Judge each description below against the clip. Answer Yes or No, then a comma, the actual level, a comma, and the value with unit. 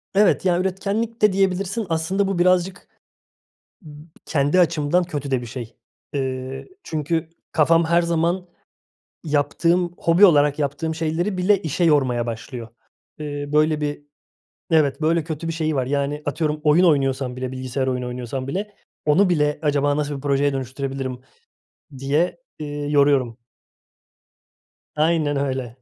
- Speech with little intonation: No, average, 3.8 semitones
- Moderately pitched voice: Yes, medium, 150 Hz